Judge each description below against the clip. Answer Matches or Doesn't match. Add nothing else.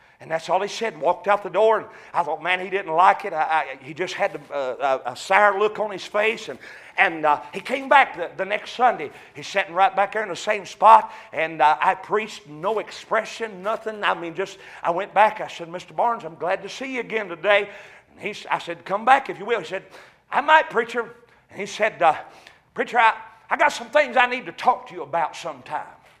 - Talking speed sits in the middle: Doesn't match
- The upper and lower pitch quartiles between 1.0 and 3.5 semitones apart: Doesn't match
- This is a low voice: Doesn't match